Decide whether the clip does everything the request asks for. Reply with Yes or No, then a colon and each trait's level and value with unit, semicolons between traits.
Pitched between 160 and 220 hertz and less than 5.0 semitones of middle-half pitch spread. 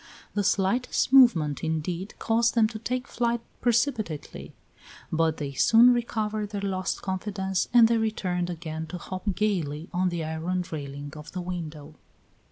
No: medium, 185 Hz; wide, 5.5 semitones